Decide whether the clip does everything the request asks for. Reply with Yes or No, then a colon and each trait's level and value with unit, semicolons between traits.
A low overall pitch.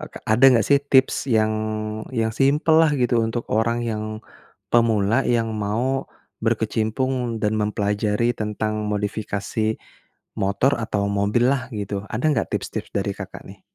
Yes: low, 110 Hz